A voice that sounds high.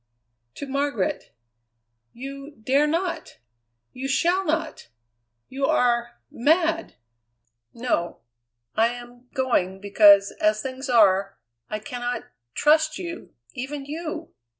Yes: very high, 260 Hz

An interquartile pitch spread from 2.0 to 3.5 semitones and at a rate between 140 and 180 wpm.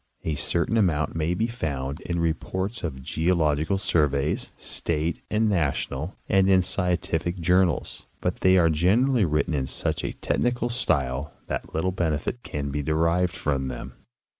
No: average, 4.1 semitones; average, 155 wpm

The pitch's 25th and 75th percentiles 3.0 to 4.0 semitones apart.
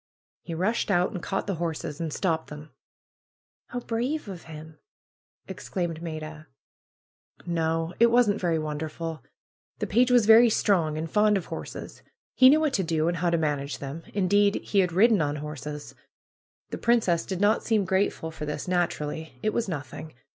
No: average, 4.7 semitones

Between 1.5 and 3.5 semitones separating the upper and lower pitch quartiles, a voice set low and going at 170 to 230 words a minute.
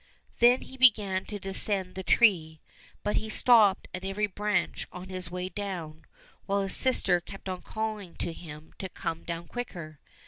No: average, 3.1 semitones; high, 190 Hz; average, 175 wpm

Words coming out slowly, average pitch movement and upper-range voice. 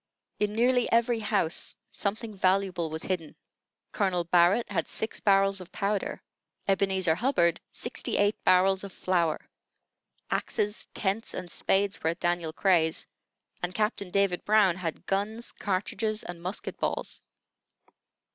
Yes: slow, 130 wpm; average, 3.0 semitones; high, 195 Hz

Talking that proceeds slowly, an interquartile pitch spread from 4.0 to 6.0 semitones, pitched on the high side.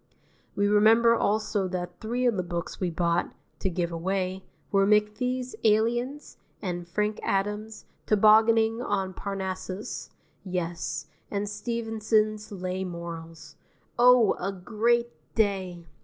No: slow, 115 wpm; average, 3.3 semitones; high, 205 Hz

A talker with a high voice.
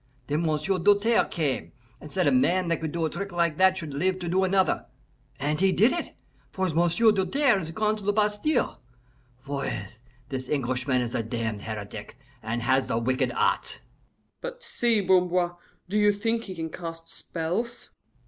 No: medium, 175 Hz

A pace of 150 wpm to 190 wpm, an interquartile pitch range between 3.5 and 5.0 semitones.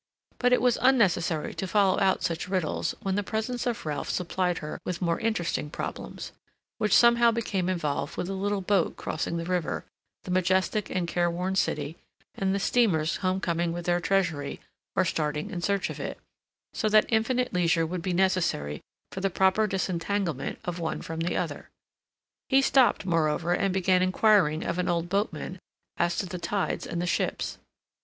No: average, 175 wpm; average, 2.9 semitones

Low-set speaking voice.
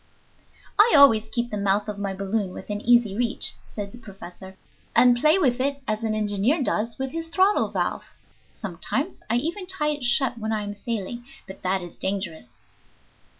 No: high, 220 Hz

